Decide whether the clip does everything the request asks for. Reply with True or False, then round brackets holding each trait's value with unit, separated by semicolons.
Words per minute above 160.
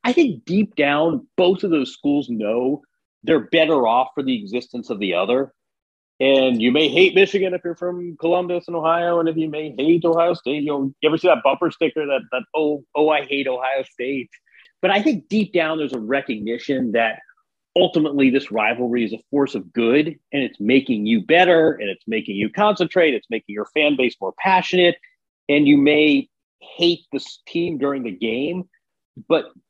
True (195 wpm)